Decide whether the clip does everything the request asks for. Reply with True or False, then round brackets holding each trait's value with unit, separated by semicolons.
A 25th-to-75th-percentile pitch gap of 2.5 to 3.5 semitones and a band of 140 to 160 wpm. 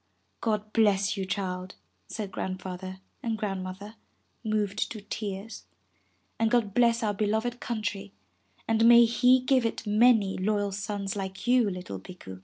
True (2.8 semitones; 145 wpm)